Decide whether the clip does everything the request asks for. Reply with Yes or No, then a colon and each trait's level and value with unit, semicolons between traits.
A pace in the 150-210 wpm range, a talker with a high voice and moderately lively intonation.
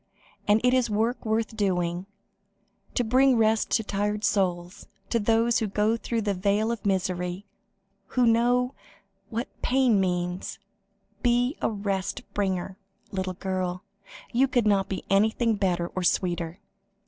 No: average, 140 wpm; high, 205 Hz; average, 3.6 semitones